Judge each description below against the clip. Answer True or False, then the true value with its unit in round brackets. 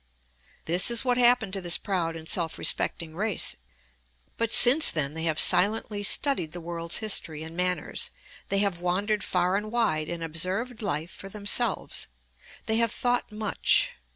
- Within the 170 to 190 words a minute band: False (160 wpm)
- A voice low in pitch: False (190 Hz)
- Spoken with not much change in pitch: False (4.8 semitones)